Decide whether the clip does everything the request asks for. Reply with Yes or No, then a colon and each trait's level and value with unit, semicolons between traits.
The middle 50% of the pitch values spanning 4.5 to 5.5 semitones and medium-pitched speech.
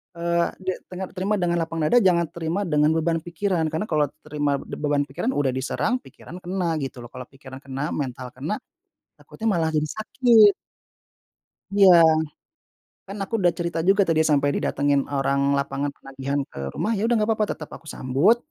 Yes: average, 4.8 semitones; medium, 160 Hz